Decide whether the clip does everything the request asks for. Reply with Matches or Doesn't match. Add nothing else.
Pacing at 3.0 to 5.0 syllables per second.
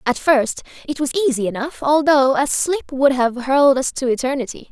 Doesn't match